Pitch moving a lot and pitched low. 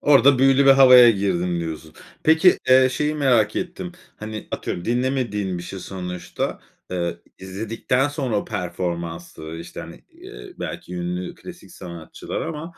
Yes: wide, 7.2 semitones; low, 105 Hz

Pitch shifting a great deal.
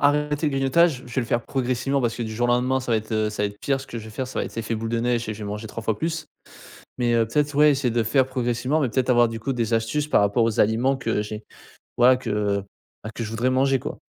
No: average, 3.1 semitones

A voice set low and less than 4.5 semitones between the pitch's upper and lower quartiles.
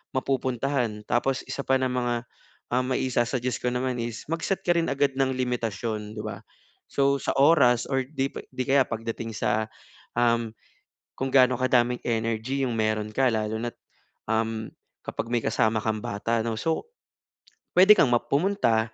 Yes: low, 120 Hz; average, 2.9 semitones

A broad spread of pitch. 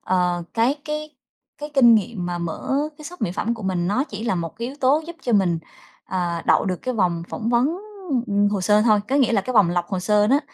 Yes: wide, 5.9 semitones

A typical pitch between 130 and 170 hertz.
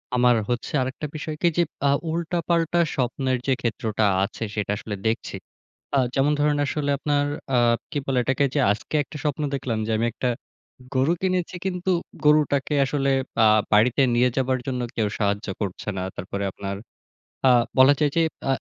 Yes: low, 135 Hz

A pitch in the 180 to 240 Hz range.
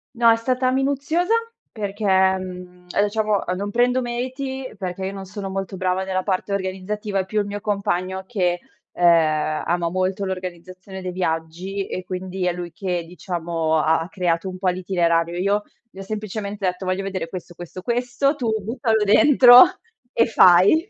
Yes: high, 190 Hz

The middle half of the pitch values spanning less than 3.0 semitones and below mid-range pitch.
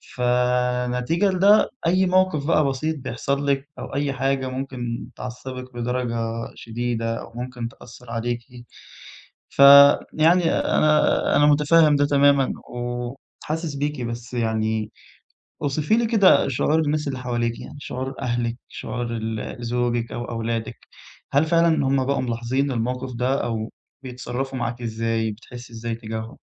No: average, 3.3 semitones; low, 125 Hz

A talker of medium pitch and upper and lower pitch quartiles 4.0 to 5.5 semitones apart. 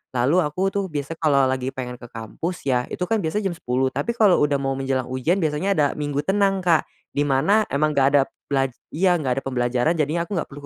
Yes: medium, 145 Hz; average, 5.0 semitones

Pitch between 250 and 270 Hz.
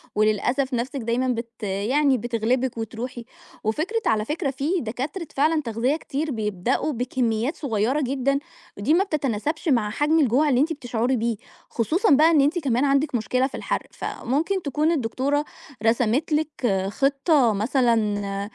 Yes: very high, 260 Hz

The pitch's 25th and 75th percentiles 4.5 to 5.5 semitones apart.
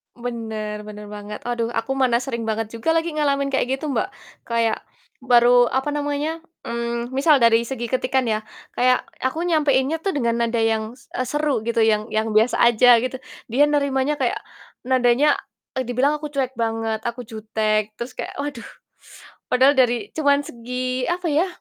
No: average, 3.5 semitones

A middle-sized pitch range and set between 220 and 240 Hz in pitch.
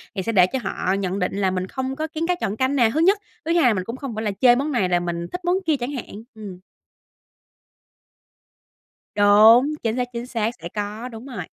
Yes: average, 5.0 semitones; high, 230 Hz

